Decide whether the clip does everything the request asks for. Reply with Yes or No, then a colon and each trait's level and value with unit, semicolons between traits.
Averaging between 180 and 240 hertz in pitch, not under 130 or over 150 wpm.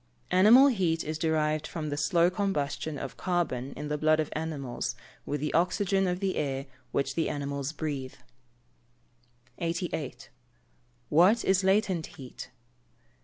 No: medium, 160 Hz; average, 140 wpm